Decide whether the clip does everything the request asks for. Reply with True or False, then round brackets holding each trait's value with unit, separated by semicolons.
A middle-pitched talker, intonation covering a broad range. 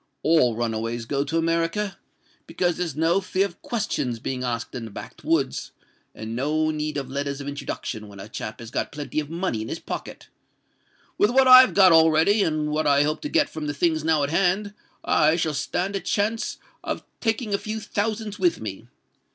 True (155 Hz; 5.9 semitones)